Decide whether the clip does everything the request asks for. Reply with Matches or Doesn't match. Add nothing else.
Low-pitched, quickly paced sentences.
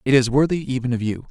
Matches